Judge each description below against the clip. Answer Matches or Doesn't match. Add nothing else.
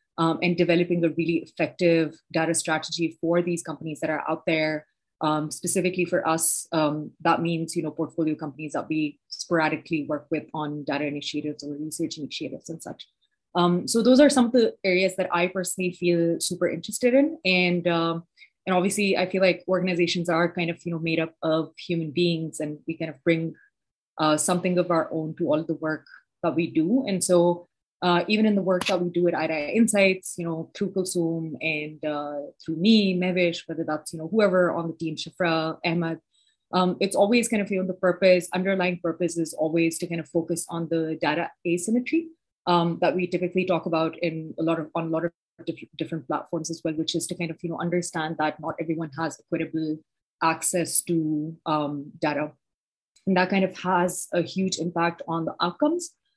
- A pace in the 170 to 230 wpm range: Matches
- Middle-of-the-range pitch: Matches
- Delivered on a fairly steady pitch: Matches